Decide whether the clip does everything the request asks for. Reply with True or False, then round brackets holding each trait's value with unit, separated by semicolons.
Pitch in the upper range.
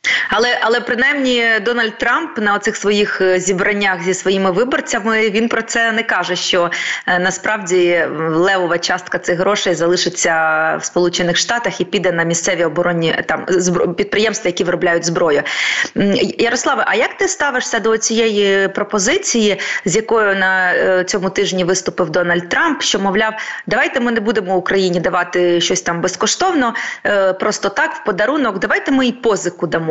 True (195 Hz)